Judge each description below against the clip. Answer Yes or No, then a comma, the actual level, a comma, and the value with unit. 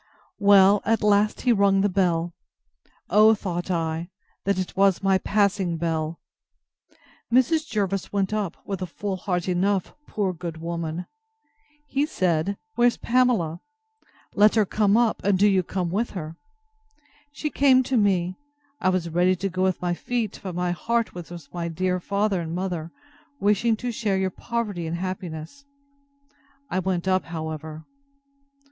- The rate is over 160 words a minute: No, average, 155 wpm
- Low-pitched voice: No, high, 190 Hz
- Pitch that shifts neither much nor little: Yes, average, 3.2 semitones